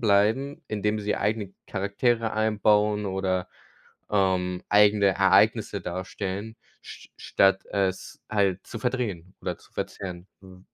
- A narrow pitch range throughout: Yes, narrow, 2.2 semitones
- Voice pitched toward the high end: No, low, 100 Hz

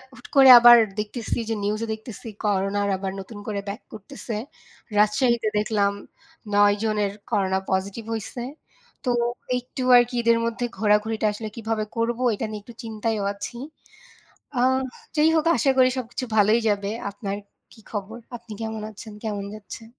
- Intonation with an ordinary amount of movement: No, narrow, 2.3 semitones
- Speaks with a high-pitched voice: Yes, high, 220 Hz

